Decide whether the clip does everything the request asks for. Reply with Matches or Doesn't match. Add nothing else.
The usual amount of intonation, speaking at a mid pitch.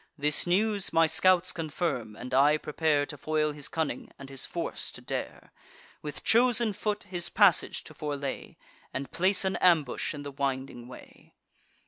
Matches